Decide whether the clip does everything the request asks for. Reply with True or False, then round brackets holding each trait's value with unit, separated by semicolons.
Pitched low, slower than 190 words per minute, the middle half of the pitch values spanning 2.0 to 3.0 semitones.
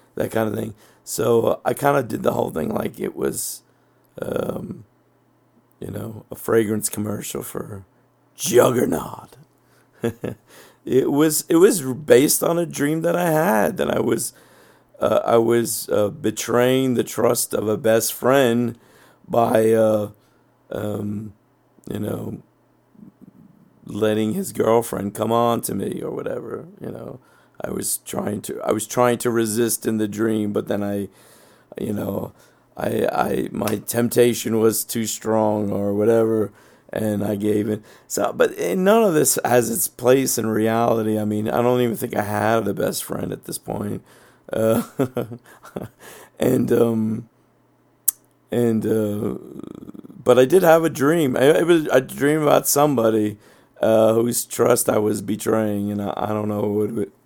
True (115 Hz; 155 wpm; 2.6 semitones)